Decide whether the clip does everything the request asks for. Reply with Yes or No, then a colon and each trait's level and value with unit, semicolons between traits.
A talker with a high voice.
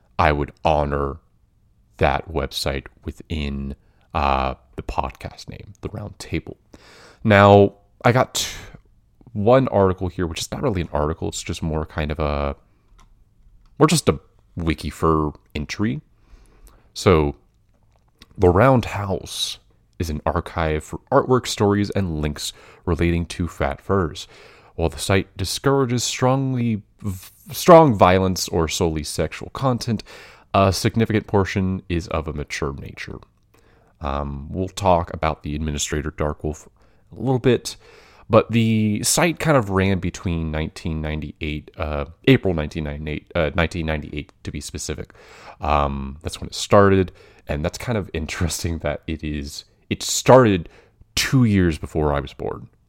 No: very low, 90 Hz